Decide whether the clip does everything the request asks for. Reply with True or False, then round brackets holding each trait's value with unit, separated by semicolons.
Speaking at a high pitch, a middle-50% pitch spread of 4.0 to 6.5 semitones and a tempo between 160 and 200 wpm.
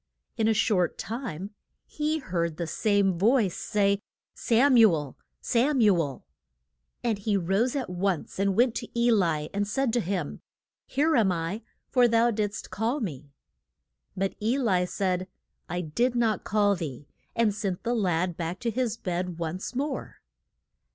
True (205 Hz; 4.8 semitones; 165 wpm)